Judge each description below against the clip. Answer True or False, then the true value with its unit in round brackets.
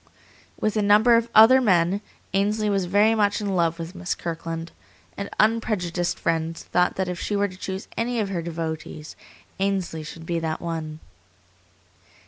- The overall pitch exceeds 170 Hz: True (185 Hz)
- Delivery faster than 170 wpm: False (165 wpm)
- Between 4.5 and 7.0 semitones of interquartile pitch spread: False (3.8 semitones)